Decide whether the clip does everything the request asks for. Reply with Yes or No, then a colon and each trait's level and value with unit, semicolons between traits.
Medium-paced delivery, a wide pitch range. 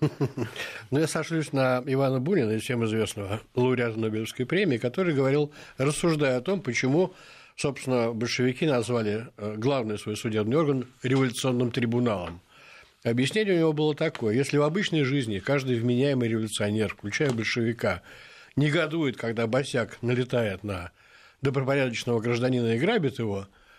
No: average, 130 wpm; average, 3.8 semitones